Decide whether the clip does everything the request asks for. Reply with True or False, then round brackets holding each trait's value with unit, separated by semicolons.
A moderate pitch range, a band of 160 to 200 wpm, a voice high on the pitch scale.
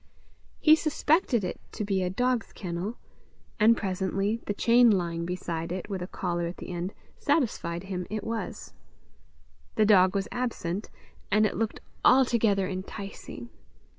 False (4.2 semitones; 145 wpm; 200 Hz)